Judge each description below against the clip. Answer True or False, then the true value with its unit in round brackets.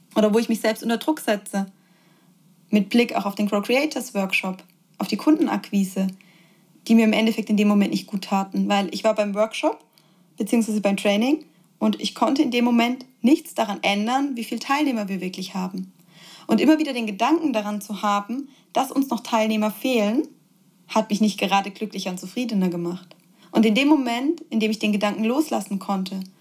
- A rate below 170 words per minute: False (190 wpm)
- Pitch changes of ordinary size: True (3.8 semitones)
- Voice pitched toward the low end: False (210 Hz)